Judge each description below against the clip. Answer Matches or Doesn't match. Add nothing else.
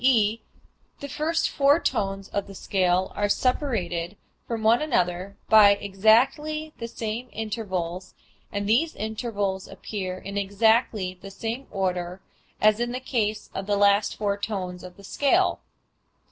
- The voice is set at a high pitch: Matches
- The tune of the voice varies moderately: Matches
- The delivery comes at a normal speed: Matches